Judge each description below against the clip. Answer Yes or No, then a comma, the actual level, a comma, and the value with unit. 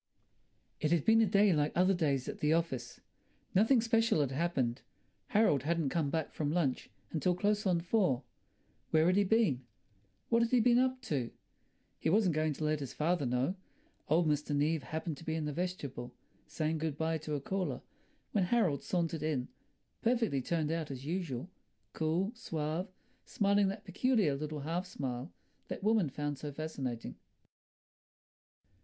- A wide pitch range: No, average, 4.7 semitones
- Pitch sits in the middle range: Yes, medium, 160 Hz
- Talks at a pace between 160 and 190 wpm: Yes, average, 170 wpm